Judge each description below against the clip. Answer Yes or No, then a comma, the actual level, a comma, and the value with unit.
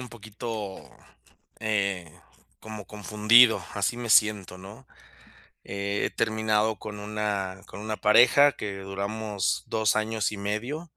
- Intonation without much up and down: Yes, narrow, 1.6 semitones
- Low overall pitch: Yes, low, 105 Hz